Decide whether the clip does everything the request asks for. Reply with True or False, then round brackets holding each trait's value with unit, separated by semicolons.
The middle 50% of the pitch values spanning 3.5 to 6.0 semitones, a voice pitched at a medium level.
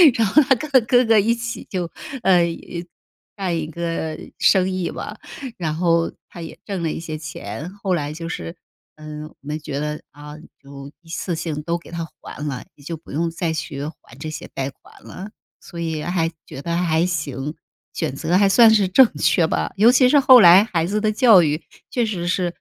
True (3.9 semitones; 170 Hz)